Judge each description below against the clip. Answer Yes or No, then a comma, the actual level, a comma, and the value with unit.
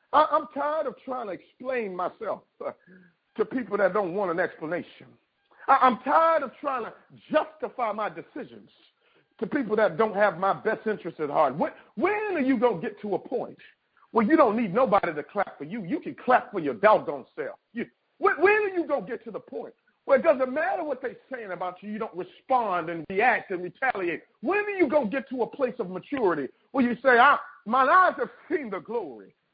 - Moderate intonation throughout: No, wide, 6.2 semitones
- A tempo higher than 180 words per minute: Yes, fast, 205 wpm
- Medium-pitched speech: No, very high, 255 Hz